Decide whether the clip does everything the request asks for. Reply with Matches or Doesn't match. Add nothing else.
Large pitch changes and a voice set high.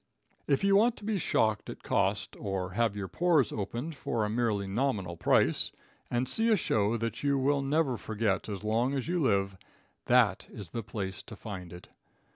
Doesn't match